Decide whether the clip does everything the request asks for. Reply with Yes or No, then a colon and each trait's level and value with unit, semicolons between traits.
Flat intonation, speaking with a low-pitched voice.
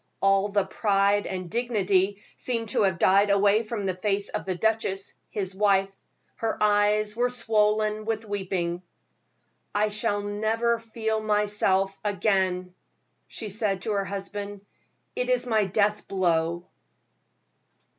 No: narrow, 1.8 semitones; high, 205 Hz